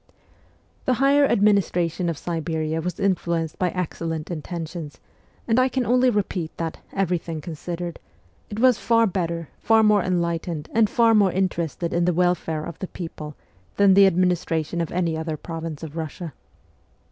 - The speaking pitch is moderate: Yes, medium, 175 Hz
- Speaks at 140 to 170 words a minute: Yes, average, 160 wpm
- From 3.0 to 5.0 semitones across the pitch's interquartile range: Yes, average, 3.4 semitones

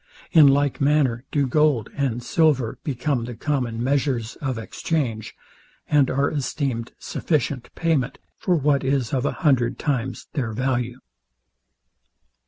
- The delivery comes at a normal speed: No, slow, 130 wpm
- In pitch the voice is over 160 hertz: No, low, 135 Hz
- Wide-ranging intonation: No, average, 3.1 semitones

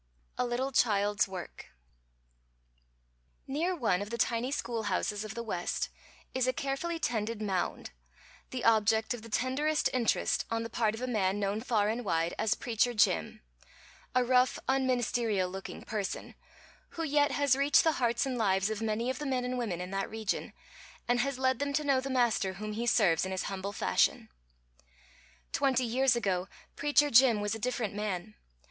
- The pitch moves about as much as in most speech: Yes, average, 3.9 semitones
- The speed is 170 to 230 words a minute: Yes, average, 180 wpm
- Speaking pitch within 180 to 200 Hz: No, high, 230 Hz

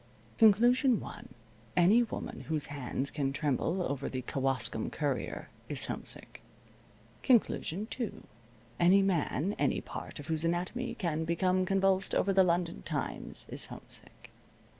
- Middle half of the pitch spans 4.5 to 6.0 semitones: Yes, average, 5.3 semitones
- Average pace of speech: No, slow, 130 wpm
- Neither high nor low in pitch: Yes, medium, 175 Hz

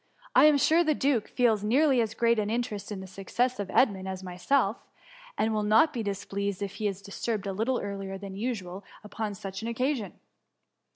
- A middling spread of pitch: Yes, average, 3.7 semitones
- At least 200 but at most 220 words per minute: Yes, fast, 205 wpm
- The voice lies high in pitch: Yes, high, 210 Hz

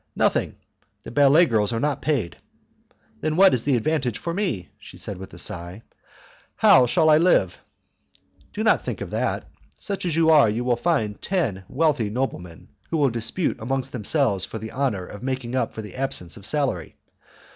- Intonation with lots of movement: Yes, wide, 6.4 semitones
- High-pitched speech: No, low, 125 Hz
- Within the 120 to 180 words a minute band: No, average, 190 wpm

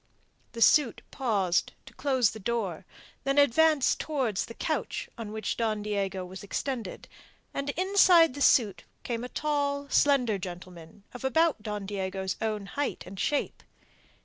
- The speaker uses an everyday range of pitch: No, wide, 6.2 semitones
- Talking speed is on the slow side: No, average, 145 wpm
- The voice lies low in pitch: No, high, 230 Hz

